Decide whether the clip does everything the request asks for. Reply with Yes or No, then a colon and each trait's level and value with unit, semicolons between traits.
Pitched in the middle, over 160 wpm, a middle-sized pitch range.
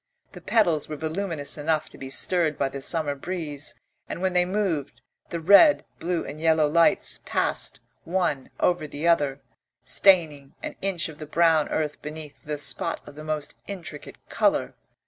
Yes: medium, 155 Hz; average, 170 wpm; average, 3.1 semitones